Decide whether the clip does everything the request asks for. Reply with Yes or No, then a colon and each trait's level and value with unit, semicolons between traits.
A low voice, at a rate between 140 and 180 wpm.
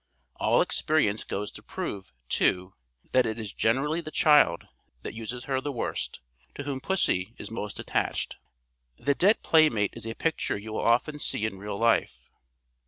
Yes: low, 115 Hz; average, 170 wpm